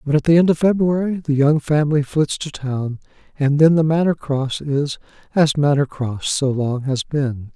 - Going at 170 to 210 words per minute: Yes, average, 200 wpm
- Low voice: No, medium, 145 Hz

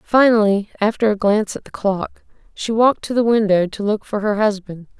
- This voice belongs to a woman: Yes, female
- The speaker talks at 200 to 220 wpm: Yes, fast, 205 wpm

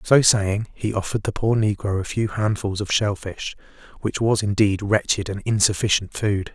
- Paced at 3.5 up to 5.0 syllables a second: Yes, 4.9 syllables/s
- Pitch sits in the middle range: No, low, 105 Hz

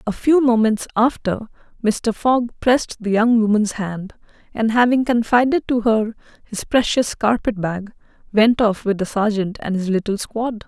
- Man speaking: No, female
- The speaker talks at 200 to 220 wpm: No, average, 165 wpm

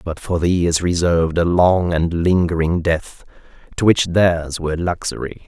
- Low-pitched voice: Yes, very low, 85 Hz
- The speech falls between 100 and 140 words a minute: No, average, 165 wpm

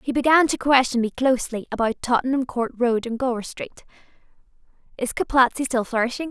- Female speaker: Yes, female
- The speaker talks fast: No, average, 160 wpm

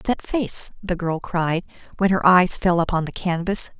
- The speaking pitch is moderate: Yes, medium, 180 Hz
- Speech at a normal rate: Yes, average, 190 wpm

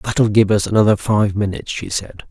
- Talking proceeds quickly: Yes, fast, 210 wpm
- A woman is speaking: No, male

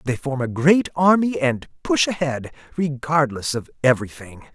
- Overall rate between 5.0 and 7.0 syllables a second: No, 4.6 syllables/s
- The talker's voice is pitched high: No, medium, 140 Hz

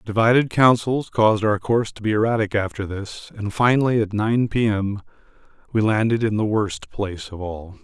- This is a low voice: Yes, low, 105 Hz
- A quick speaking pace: No, average, 185 wpm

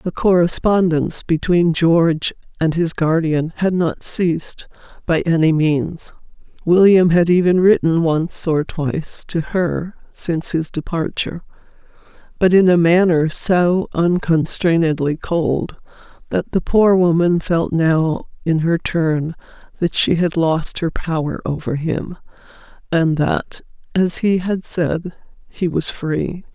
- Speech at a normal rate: No, slow, 130 wpm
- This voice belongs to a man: No, female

